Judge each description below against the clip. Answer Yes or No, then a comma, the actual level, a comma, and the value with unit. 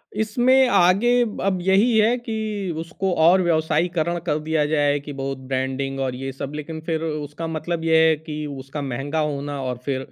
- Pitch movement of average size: Yes, average, 4.6 semitones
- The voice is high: No, medium, 155 Hz